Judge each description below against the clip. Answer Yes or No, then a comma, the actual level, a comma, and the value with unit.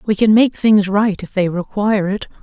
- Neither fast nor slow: No, fast, 225 wpm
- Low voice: No, high, 205 Hz